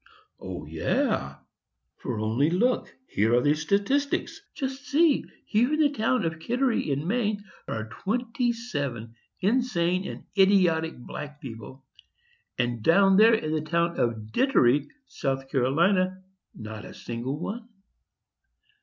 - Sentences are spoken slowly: Yes, slow, 130 wpm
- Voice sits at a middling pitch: Yes, medium, 170 Hz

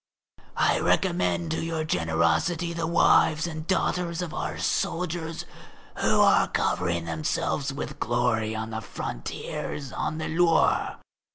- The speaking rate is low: Yes, slow, 130 wpm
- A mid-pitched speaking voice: Yes, medium, 150 Hz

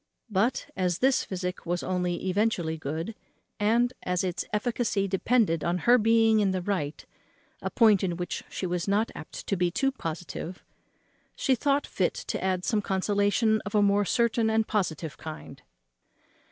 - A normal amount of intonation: Yes, average, 3.9 semitones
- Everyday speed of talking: Yes, average, 165 wpm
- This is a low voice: No, high, 195 Hz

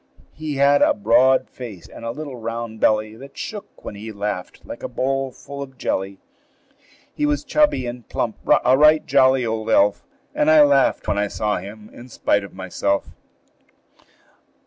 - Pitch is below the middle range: Yes, low, 120 Hz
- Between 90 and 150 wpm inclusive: No, average, 170 wpm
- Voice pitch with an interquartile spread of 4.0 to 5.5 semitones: Yes, average, 4.7 semitones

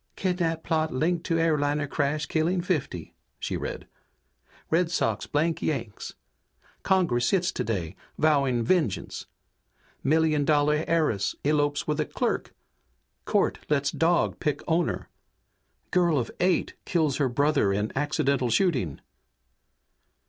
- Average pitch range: Yes, average, 3.2 semitones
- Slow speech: Yes, slow, 120 wpm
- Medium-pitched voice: Yes, medium, 150 Hz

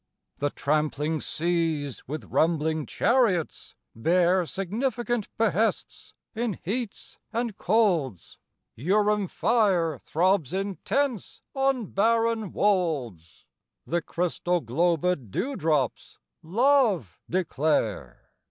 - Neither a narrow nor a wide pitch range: No, wide, 6.0 semitones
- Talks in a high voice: No, medium, 180 Hz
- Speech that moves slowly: Yes, slow, 90 wpm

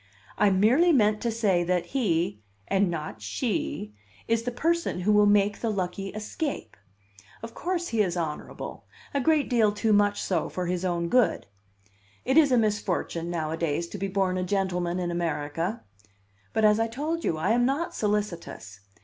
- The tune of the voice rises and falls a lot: No, average, 4.9 semitones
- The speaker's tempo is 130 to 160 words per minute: No, average, 175 wpm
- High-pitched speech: Yes, high, 200 Hz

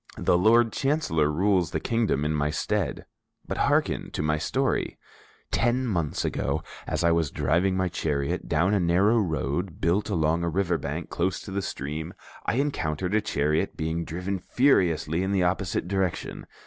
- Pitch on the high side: No, very low, 90 Hz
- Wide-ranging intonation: No, average, 4.1 semitones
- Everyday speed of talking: Yes, average, 170 wpm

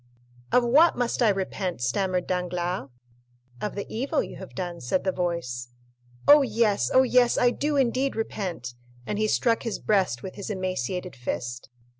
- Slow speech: No, average, 165 wpm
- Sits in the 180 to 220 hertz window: Yes, high, 190 Hz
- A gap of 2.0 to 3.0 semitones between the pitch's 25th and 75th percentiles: No, average, 5.1 semitones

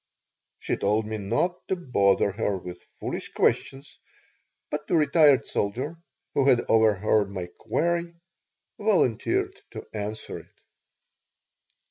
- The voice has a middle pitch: No, low, 125 Hz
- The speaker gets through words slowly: Yes, slow, 115 wpm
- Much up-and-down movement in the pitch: Yes, wide, 8.6 semitones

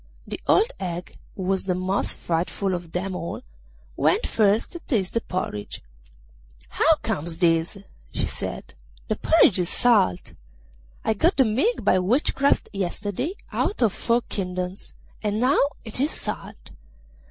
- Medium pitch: No, high, 195 Hz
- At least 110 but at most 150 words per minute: Yes, average, 145 wpm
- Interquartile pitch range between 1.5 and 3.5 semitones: No, average, 4.6 semitones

